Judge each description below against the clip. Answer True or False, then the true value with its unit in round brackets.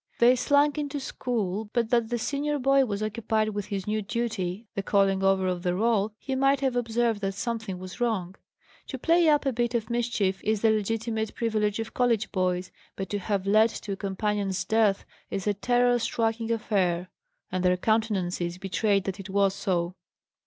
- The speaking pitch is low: False (215 Hz)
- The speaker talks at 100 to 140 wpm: False (190 wpm)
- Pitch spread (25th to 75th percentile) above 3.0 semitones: True (3.4 semitones)